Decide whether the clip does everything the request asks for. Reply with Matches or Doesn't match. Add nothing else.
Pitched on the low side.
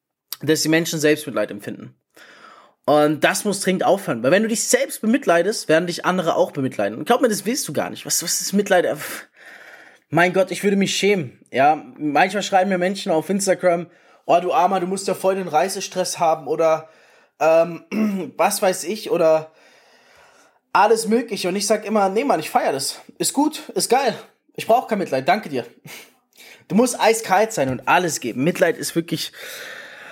Doesn't match